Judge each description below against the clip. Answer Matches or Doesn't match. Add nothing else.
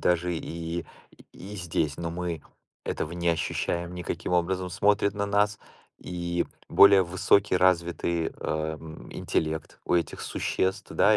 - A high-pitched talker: Doesn't match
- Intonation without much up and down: Matches